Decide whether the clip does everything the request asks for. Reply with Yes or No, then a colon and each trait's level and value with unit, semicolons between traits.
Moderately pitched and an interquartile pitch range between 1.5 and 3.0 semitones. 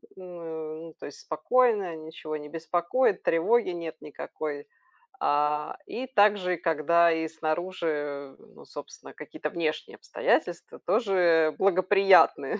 No: medium, 165 Hz; average, 3.4 semitones